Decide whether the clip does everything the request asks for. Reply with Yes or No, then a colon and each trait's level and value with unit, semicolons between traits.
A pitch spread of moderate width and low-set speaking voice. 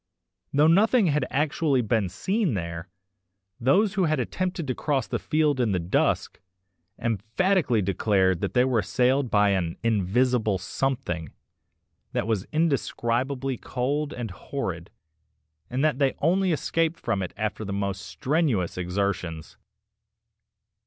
No: wide, 7.1 semitones; low, 125 Hz